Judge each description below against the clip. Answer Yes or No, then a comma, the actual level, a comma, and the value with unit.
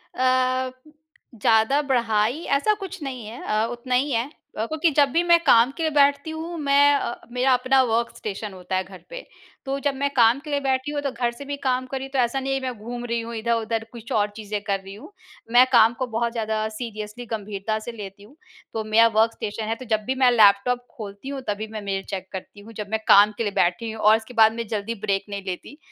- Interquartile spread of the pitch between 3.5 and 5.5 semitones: Yes, average, 3.8 semitones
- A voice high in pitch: Yes, high, 235 Hz